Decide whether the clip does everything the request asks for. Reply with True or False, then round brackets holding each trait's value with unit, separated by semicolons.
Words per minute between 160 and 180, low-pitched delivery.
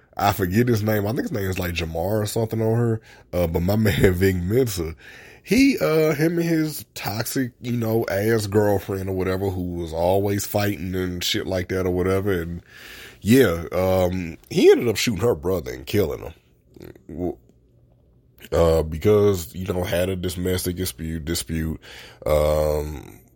True (165 wpm; 95 Hz)